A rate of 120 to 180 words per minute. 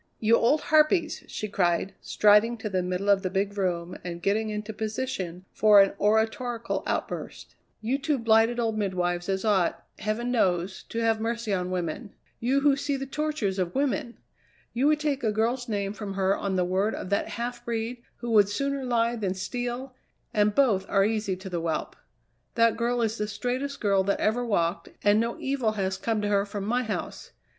No: average, 195 wpm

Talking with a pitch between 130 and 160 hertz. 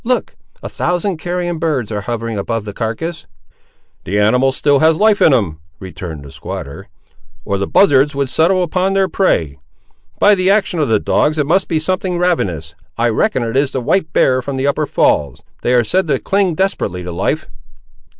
Yes: medium, 140 Hz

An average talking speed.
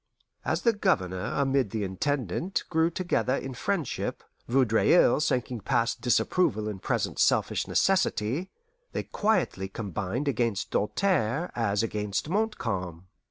No: slow, 115 wpm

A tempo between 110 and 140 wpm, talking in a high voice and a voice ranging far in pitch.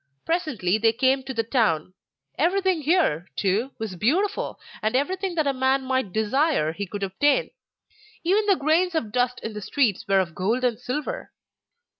No: average, 170 wpm; very high, 255 Hz; wide, 7.2 semitones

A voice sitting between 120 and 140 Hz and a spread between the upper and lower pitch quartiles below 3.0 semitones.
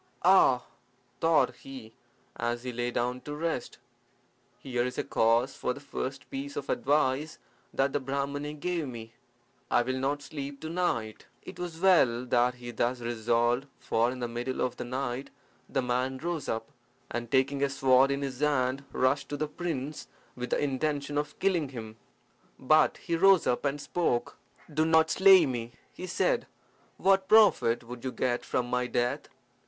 No: low, 135 Hz; average, 3.5 semitones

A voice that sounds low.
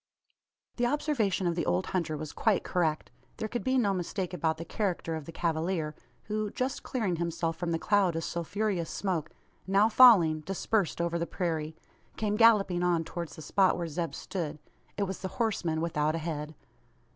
No: medium, 175 Hz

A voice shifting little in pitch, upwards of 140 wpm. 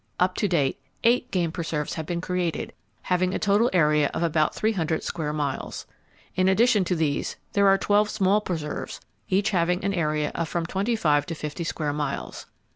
No: average, 4.2 semitones; average, 190 wpm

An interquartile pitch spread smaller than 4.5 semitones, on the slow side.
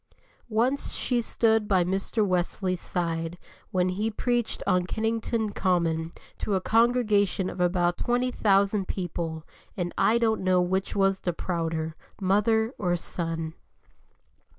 Yes: average, 3.9 semitones; slow, 130 wpm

